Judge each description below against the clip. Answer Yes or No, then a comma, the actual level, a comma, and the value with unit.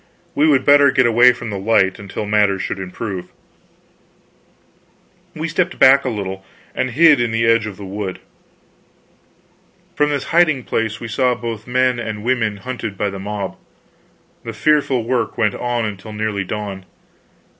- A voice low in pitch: Yes, low, 115 Hz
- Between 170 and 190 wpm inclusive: No, average, 160 wpm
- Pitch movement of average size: Yes, average, 3.9 semitones